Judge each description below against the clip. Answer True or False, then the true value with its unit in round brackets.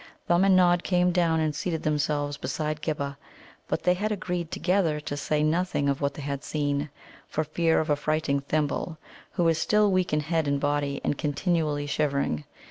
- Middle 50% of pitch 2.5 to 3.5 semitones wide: True (3.1 semitones)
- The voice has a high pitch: False (155 Hz)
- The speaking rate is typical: True (185 wpm)